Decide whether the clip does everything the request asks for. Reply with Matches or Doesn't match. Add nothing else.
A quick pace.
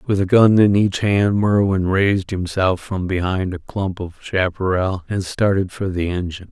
Doesn't match